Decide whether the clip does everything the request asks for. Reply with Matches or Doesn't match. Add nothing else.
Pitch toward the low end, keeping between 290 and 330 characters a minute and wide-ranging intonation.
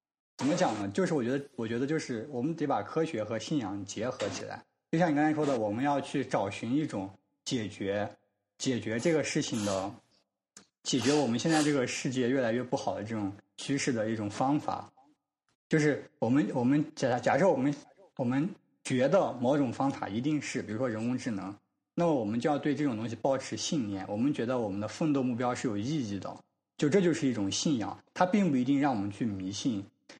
Matches